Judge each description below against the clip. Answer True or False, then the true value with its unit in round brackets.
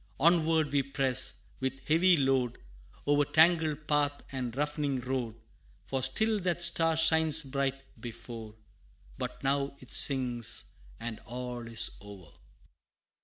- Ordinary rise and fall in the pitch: True (3.9 semitones)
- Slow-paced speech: True (120 wpm)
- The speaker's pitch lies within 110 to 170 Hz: True (135 Hz)